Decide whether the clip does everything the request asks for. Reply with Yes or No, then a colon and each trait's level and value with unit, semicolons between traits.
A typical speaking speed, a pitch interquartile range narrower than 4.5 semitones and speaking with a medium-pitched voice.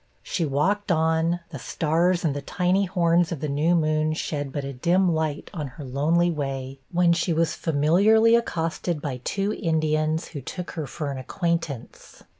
Yes: average, 175 wpm; average, 3.1 semitones; medium, 160 Hz